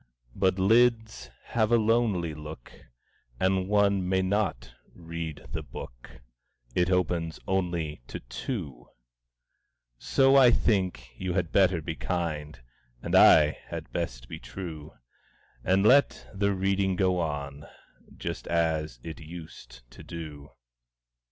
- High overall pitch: No, very low, 90 Hz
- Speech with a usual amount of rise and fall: Yes, average, 4.1 semitones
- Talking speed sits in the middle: No, slow, 125 wpm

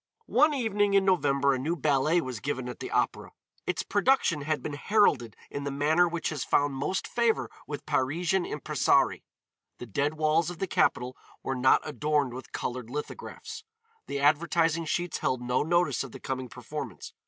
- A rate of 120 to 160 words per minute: No, average, 175 wpm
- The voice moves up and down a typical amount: Yes, average, 4.7 semitones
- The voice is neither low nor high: Yes, medium, 150 Hz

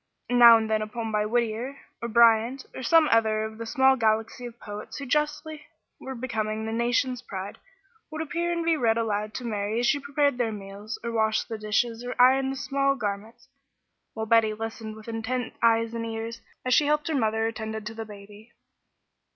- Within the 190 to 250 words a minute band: Yes, average, 200 wpm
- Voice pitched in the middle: No, high, 230 Hz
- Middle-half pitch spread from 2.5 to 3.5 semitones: Yes, average, 2.9 semitones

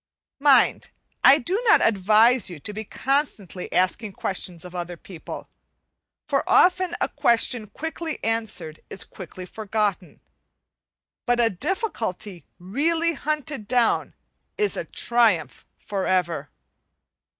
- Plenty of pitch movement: Yes, wide, 7.2 semitones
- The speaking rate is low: Yes, slow, 115 wpm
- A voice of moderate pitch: No, high, 220 Hz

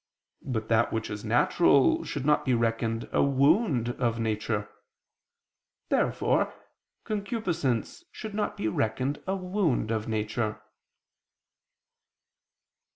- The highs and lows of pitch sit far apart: Yes, wide, 6.6 semitones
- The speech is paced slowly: Yes, slow, 105 wpm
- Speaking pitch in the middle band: No, low, 120 Hz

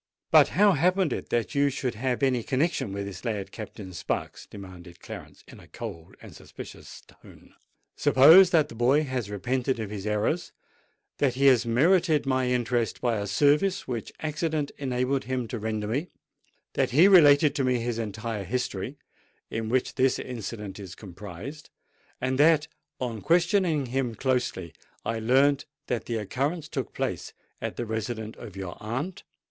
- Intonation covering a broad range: No, average, 4.8 semitones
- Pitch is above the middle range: No, low, 125 Hz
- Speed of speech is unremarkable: Yes, average, 160 wpm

